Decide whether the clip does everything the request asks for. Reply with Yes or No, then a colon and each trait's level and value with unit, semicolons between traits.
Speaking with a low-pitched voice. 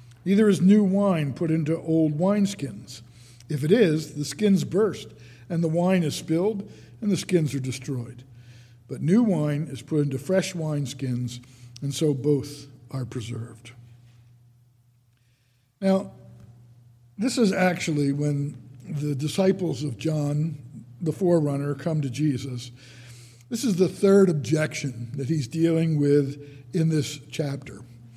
No: medium, 145 Hz